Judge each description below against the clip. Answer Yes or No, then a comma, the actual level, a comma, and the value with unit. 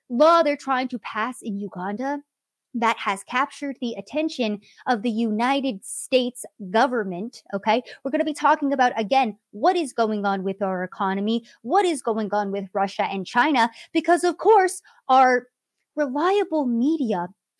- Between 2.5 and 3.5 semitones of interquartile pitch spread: No, wide, 5.5 semitones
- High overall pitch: Yes, high, 245 Hz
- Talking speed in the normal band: Yes, average, 155 wpm